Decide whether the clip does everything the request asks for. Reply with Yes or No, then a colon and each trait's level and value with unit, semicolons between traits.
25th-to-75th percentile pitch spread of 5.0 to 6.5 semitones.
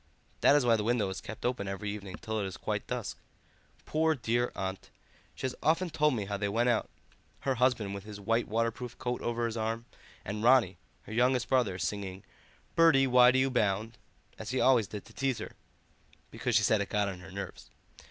No: average, 3.7 semitones